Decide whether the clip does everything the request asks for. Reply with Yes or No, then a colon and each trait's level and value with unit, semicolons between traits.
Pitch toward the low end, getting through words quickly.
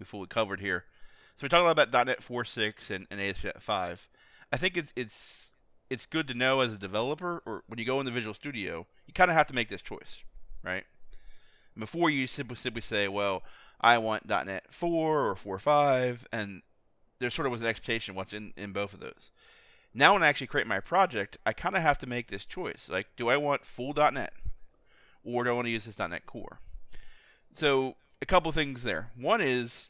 Yes: low, 125 Hz; fast, 210 wpm